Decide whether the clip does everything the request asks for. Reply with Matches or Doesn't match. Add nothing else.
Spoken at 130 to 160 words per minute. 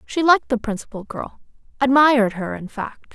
Matches